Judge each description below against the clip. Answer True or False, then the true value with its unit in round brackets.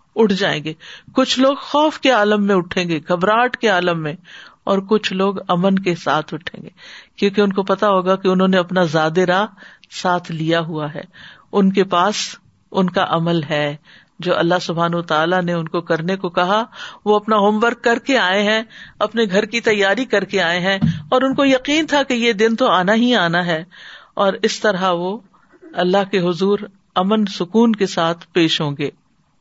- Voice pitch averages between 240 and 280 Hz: False (195 Hz)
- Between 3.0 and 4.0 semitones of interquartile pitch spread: True (3.5 semitones)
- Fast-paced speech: True (200 wpm)